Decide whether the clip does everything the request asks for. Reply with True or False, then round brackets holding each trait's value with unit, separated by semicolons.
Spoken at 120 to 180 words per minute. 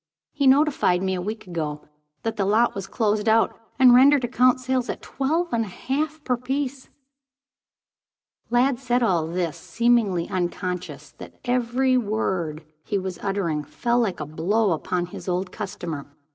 True (160 wpm)